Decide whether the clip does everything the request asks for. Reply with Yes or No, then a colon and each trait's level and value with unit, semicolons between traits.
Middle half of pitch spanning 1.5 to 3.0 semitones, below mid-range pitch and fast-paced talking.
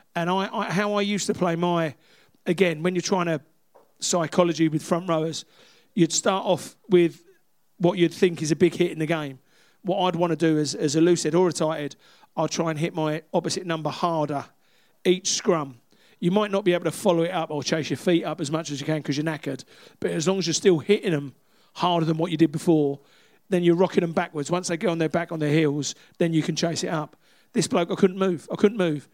No: narrow, 2.5 semitones; medium, 170 Hz; fast, 245 wpm